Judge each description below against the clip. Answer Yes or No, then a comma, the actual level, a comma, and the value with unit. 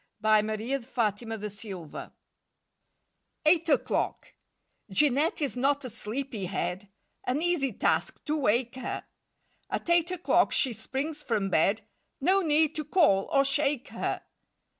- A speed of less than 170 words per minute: Yes, average, 145 wpm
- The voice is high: Yes, very high, 260 Hz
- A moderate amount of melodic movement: No, wide, 6.0 semitones